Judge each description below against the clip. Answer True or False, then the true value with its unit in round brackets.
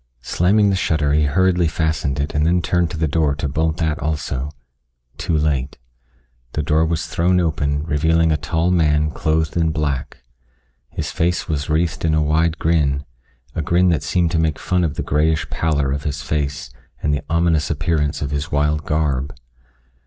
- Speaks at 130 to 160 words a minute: False (180 wpm)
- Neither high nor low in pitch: False (80 Hz)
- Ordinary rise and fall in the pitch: False (2.2 semitones)